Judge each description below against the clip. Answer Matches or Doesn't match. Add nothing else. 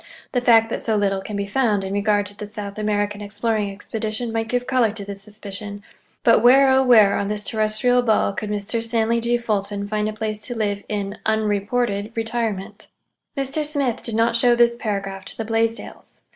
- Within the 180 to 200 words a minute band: Matches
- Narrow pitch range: Matches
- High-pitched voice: Matches